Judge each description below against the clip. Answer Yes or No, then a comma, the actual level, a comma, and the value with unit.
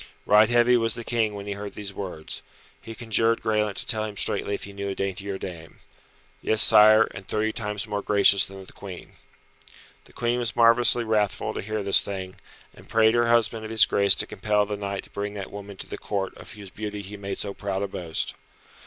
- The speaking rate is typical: No, fast, 220 wpm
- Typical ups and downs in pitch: No, narrow, 1.8 semitones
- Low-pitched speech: Yes, low, 105 Hz